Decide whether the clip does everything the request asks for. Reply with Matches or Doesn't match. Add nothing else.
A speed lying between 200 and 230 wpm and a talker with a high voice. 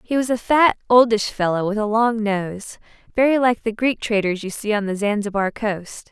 Matches